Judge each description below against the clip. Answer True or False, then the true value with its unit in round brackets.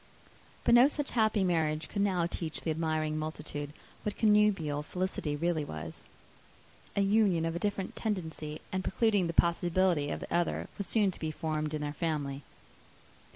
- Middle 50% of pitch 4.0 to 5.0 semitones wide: True (4.4 semitones)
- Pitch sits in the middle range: True (170 Hz)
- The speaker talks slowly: False (165 wpm)